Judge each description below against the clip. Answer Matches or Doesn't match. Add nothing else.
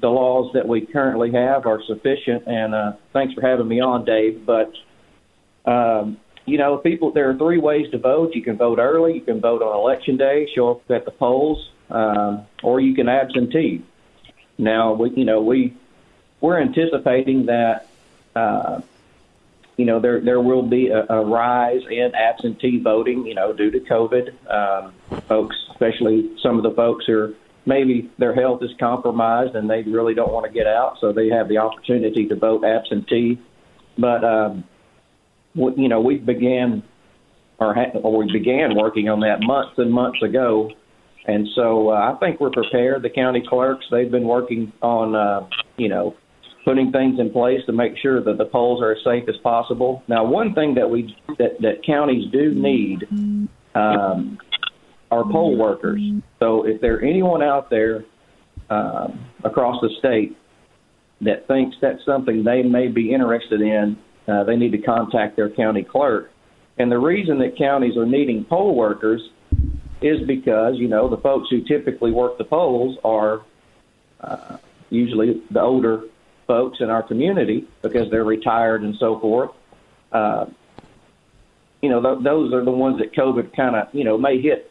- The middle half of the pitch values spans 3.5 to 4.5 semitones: Doesn't match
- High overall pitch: Doesn't match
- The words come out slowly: Doesn't match